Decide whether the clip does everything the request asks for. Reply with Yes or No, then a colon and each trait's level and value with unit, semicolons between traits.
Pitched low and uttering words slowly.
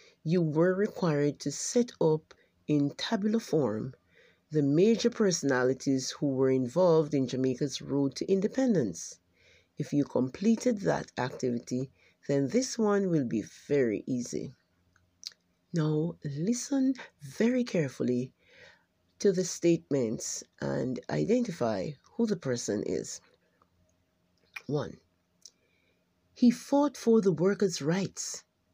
No: medium, 150 Hz; slow, 110 wpm